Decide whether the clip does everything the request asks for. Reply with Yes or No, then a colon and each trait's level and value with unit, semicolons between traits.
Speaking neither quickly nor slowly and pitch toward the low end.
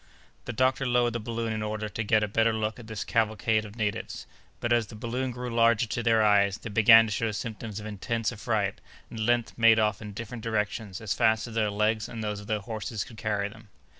No: fast, 235 wpm; low, 110 Hz